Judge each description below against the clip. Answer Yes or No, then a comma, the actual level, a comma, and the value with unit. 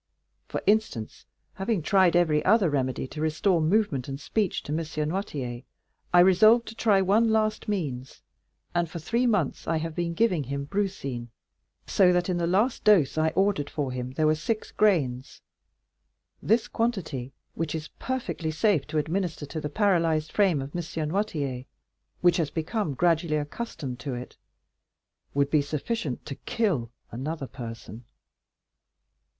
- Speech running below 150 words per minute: No, average, 155 wpm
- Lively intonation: Yes, wide, 5.7 semitones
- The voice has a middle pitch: Yes, medium, 165 Hz